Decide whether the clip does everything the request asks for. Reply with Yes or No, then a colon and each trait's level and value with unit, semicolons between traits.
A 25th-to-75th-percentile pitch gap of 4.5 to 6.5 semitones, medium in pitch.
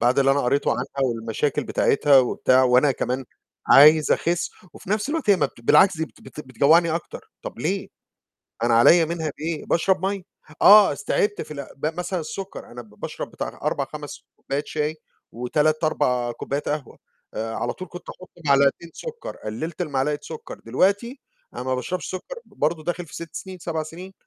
Yes: average, 5.1 semitones; medium, 155 Hz